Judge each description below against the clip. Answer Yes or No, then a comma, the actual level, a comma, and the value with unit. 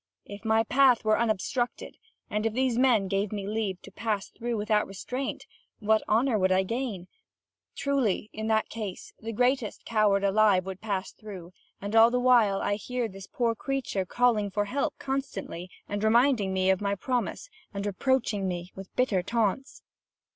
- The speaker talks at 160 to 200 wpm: Yes, average, 170 wpm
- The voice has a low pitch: No, high, 215 Hz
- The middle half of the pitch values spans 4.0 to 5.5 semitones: No, average, 3.6 semitones